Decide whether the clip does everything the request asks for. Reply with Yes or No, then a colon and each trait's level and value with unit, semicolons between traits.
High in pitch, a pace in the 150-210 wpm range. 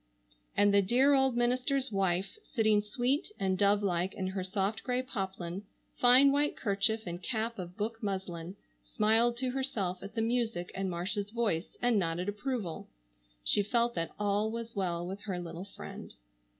Yes: high, 205 Hz; average, 165 wpm